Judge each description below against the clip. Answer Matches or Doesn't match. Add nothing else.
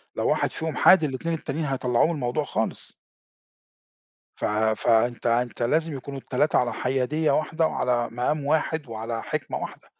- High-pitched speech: Doesn't match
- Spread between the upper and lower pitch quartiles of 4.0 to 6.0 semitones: Matches